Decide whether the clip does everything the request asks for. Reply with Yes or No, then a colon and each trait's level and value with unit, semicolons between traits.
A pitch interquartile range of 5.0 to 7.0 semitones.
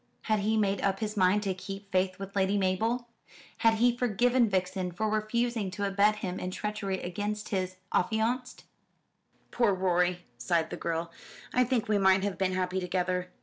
No: average, 2.7 semitones